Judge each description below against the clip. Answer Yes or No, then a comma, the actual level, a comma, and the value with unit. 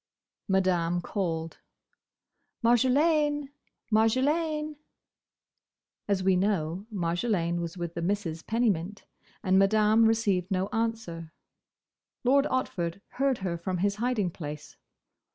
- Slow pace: Yes, slow, 100 wpm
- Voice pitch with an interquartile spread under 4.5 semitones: No, wide, 5.4 semitones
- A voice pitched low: No, high, 200 Hz